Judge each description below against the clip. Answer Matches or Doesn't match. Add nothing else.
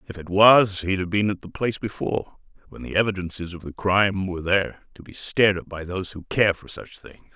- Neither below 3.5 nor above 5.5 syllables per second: Doesn't match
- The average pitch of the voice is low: Matches